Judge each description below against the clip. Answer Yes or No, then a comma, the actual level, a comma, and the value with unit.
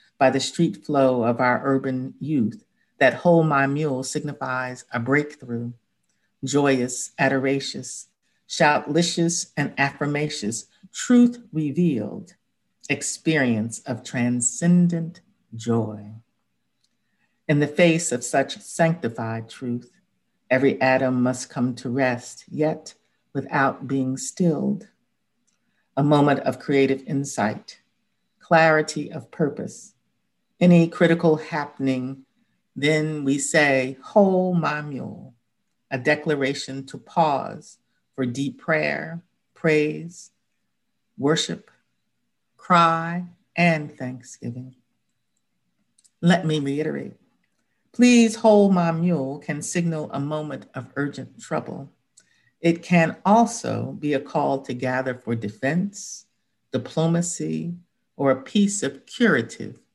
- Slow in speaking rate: Yes, slow, 105 wpm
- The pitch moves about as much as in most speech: Yes, average, 4.5 semitones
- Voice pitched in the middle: Yes, medium, 145 Hz